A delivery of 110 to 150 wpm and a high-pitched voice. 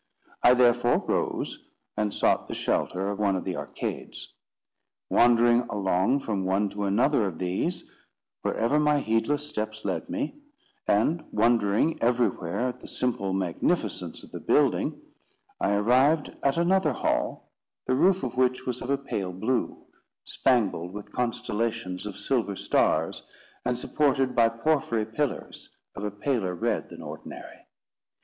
No: average, 140 wpm; low, 120 Hz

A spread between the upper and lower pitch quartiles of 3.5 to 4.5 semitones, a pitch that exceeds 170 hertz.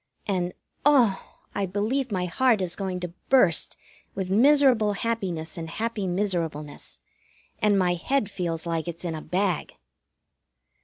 Yes: average, 4.1 semitones; high, 190 Hz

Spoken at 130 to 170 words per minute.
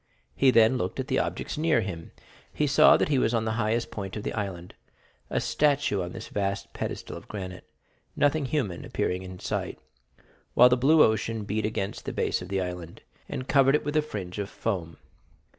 No: average, 195 wpm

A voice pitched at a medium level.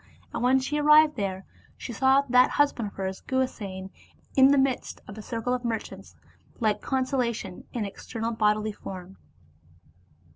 No: high, 235 Hz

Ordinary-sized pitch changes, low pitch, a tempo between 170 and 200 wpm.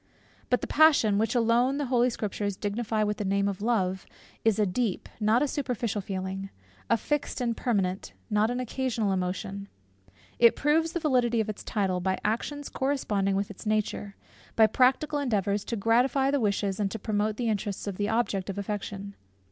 No: average, 3.6 semitones; high, 215 Hz; average, 180 wpm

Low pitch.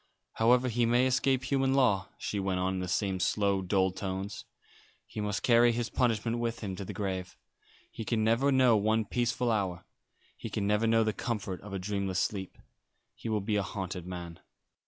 Yes: low, 105 Hz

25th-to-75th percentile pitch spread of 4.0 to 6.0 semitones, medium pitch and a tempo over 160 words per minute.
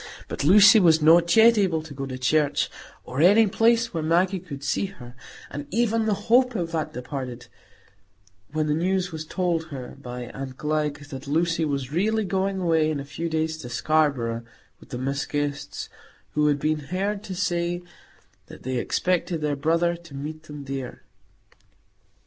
Yes: average, 4.4 semitones; medium, 155 Hz; average, 175 wpm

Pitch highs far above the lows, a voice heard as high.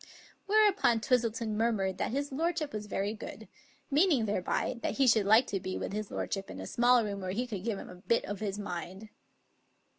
No: average, 4.1 semitones; high, 220 Hz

